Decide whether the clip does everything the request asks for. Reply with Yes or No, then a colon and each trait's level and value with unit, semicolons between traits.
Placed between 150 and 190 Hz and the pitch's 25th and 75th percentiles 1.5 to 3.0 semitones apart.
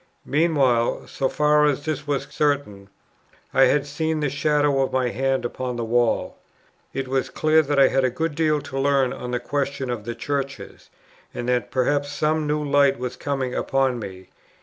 No: low, 135 Hz; narrow, 2.6 semitones